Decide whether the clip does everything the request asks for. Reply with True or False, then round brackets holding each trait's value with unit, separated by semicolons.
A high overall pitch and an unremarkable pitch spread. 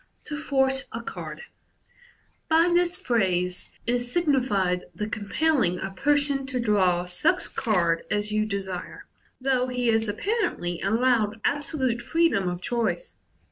False (235 Hz; 6.4 semitones)